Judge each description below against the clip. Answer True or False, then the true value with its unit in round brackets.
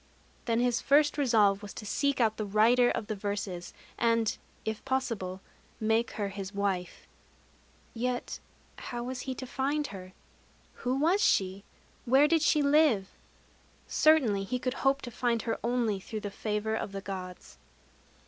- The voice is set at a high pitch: True (230 Hz)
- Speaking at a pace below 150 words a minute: False (160 wpm)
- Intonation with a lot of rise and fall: False (4.4 semitones)